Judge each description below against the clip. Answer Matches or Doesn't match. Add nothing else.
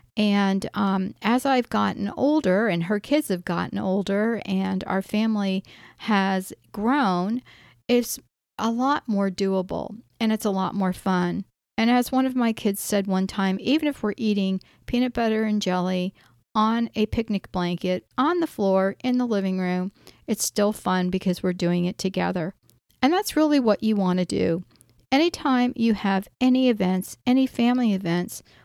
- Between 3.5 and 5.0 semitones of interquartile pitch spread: Matches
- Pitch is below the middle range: Doesn't match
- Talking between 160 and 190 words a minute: Matches